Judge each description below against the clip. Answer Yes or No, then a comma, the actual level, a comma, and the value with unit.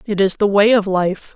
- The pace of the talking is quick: Yes, fast, 265 wpm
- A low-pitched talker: No, high, 200 Hz